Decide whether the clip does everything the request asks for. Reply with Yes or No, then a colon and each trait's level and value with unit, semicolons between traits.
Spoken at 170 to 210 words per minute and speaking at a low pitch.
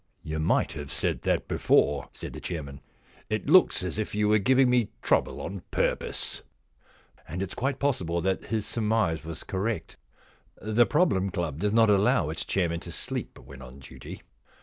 Yes: average, 185 wpm; very low, 95 Hz